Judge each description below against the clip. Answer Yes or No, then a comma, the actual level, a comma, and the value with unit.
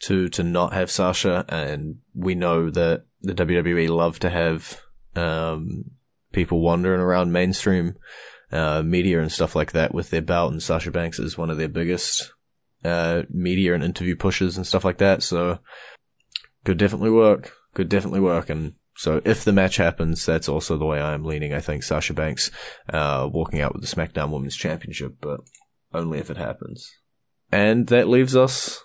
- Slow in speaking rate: No, average, 180 wpm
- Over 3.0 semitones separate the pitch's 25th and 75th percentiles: No, narrow, 2.6 semitones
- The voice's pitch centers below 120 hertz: Yes, very low, 85 Hz